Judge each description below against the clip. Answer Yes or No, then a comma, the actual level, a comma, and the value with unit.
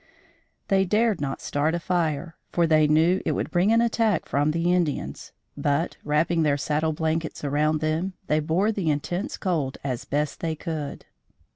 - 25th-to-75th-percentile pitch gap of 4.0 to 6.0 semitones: No, average, 3.0 semitones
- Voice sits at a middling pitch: Yes, medium, 160 Hz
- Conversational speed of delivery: Yes, average, 170 wpm